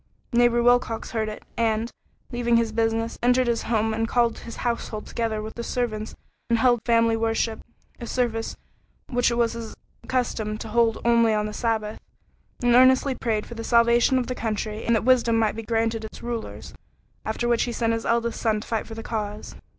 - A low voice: No, high, 230 Hz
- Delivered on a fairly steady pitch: Yes, narrow, 1.3 semitones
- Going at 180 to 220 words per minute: Yes, average, 195 wpm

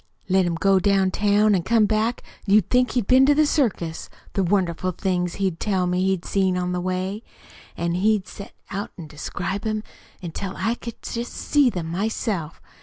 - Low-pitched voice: No, high, 195 Hz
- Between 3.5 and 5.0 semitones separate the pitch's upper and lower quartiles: No, average, 3.1 semitones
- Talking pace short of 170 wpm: No, average, 185 wpm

